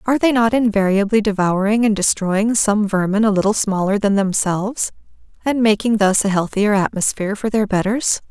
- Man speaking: No, female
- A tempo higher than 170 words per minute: No, average, 165 wpm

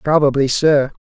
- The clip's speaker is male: Yes, male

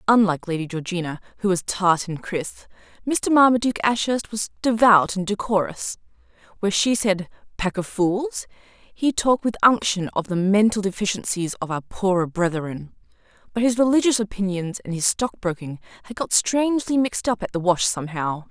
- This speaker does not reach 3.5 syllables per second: No, 5.3 syllables/s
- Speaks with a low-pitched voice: No, high, 200 Hz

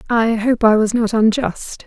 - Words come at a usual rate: Yes, average, 195 wpm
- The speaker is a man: No, female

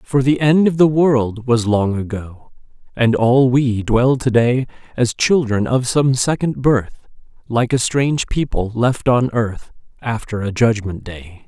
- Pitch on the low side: Yes, low, 120 Hz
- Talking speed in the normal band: Yes, average, 165 wpm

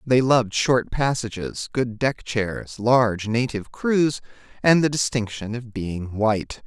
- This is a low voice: Yes, low, 120 Hz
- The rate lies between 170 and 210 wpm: No, average, 145 wpm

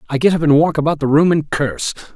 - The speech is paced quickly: Yes, fast, 280 wpm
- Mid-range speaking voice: Yes, medium, 150 Hz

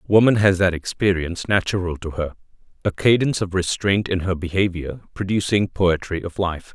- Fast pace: No, average, 150 wpm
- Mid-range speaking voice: No, very low, 95 Hz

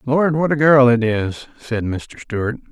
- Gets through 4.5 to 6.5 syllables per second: No, 3.9 syllables/s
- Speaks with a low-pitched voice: Yes, low, 125 Hz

